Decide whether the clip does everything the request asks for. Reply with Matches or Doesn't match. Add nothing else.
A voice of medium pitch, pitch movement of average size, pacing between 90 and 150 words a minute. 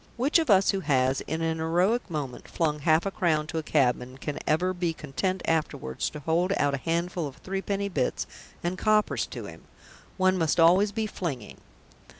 Doesn't match